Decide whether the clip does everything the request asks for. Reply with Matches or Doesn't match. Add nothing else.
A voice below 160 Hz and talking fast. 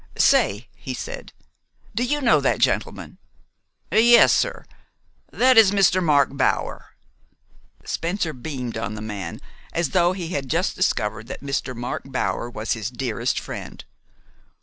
Doesn't match